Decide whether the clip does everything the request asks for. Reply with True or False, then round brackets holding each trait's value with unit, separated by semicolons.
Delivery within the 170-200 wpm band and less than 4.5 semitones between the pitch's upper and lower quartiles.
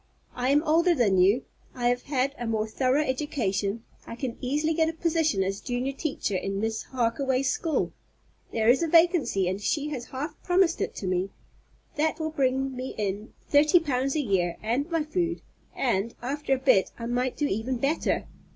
False (190 wpm; 5.2 semitones)